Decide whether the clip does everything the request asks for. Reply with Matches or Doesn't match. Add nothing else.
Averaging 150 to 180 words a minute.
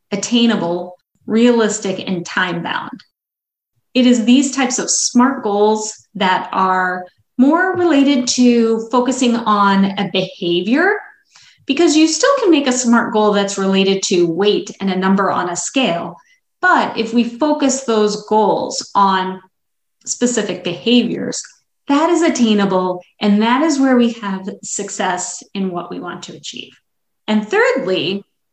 Doesn't match